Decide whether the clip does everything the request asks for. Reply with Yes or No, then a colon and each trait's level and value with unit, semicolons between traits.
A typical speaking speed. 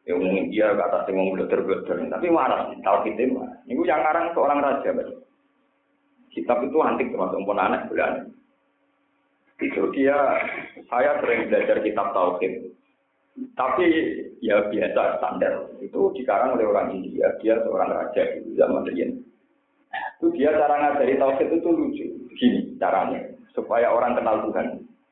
No: fast, 145 wpm